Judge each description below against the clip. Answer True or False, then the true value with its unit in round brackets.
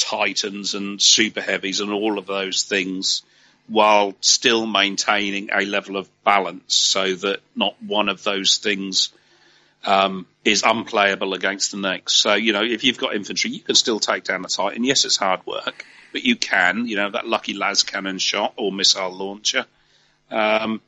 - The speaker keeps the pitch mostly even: True (1.2 semitones)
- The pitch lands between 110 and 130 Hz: False (100 Hz)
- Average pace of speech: True (175 wpm)